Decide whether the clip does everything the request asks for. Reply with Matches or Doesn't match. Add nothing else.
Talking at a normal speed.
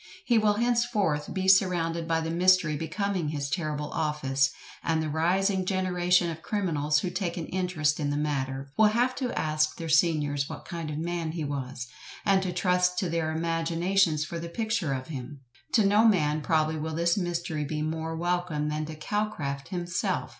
Matches